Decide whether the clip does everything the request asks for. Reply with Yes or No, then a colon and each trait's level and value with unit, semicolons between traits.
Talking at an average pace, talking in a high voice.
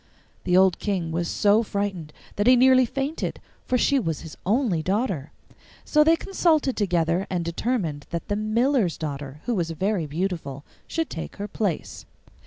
Yes: average, 165 wpm; high, 195 Hz